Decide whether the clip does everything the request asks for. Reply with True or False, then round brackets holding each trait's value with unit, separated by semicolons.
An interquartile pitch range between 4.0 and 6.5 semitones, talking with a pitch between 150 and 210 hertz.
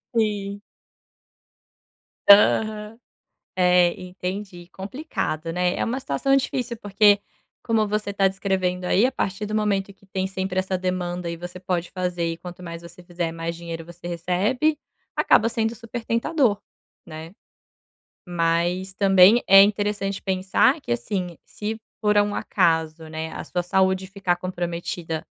False (3.0 semitones; 190 Hz)